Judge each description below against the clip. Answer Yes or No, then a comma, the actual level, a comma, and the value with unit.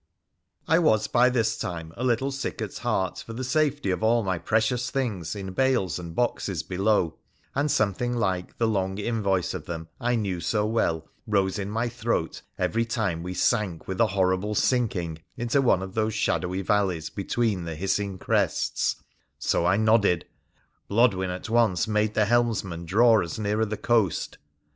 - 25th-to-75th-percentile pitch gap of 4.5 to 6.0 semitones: No, average, 4.0 semitones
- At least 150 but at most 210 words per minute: Yes, average, 175 wpm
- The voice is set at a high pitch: No, low, 105 Hz